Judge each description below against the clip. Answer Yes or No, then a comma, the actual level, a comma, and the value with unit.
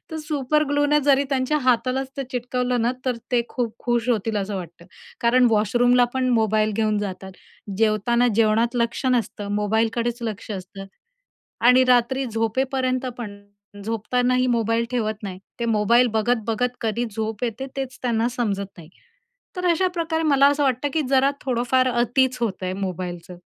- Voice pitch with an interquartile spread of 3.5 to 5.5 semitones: No, average, 3.0 semitones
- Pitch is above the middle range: Yes, high, 240 Hz